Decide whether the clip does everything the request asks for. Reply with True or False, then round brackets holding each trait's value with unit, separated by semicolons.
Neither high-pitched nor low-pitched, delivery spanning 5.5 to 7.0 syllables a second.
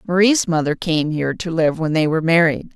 True (165 Hz; 5.8 syllables/s)